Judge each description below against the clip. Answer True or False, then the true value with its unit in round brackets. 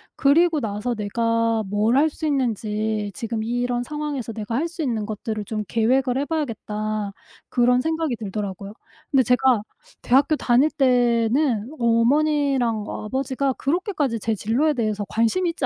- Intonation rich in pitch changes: False (4.3 semitones)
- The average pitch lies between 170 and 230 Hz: False (240 Hz)